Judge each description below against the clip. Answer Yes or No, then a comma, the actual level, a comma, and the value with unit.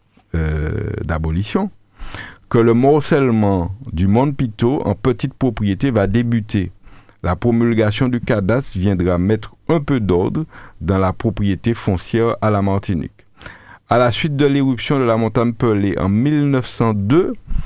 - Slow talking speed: Yes, slow, 135 wpm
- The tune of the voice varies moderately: Yes, average, 4.1 semitones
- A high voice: No, low, 110 Hz